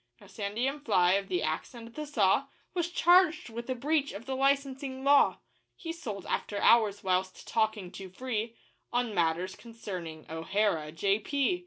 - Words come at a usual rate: Yes, average, 160 wpm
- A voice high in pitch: Yes, high, 230 Hz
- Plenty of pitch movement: Yes, wide, 6.0 semitones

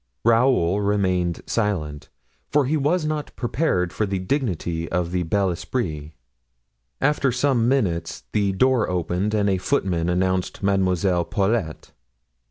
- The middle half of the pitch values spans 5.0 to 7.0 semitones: Yes, average, 5.3 semitones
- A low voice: Yes, very low, 95 Hz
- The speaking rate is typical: No, slow, 130 wpm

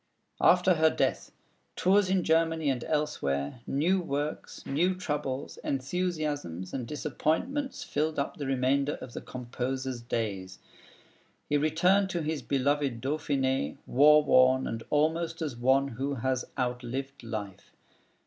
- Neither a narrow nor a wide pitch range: Yes, average, 3.7 semitones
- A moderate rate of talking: No, slow, 130 wpm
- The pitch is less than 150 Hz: Yes, medium, 140 Hz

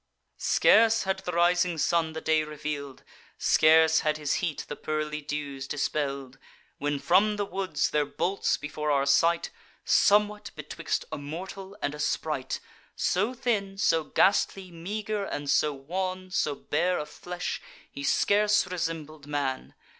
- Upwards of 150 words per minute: No, average, 145 wpm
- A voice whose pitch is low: No, medium, 160 Hz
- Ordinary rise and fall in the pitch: Yes, average, 4.3 semitones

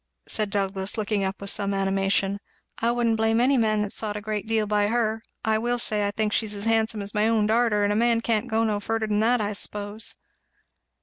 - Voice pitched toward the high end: Yes, high, 215 Hz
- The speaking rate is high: Yes, fast, 230 wpm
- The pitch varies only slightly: Yes, narrow, 1.7 semitones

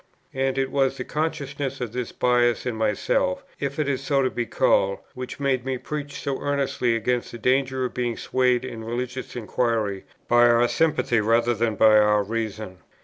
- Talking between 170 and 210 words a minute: Yes, average, 185 wpm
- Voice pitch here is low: Yes, low, 125 Hz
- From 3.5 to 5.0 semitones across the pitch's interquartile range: No, narrow, 2.6 semitones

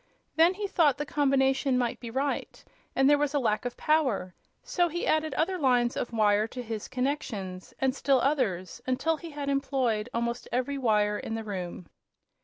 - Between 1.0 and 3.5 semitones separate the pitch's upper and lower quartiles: No, average, 4.3 semitones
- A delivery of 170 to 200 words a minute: Yes, average, 185 wpm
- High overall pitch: Yes, very high, 260 Hz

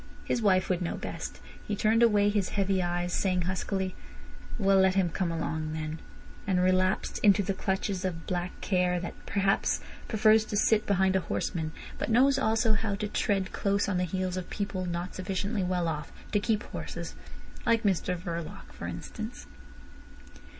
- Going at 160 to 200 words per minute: Yes, average, 170 wpm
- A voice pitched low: No, high, 190 Hz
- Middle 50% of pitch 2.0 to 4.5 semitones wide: Yes, narrow, 2.4 semitones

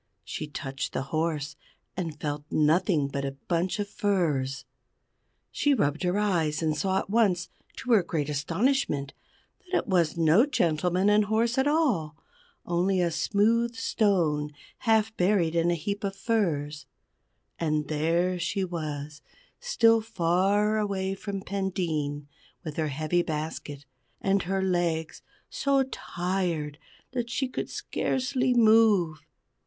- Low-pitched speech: No, medium, 180 Hz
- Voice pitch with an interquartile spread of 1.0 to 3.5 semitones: No, average, 5.2 semitones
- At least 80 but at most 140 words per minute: Yes, slow, 135 wpm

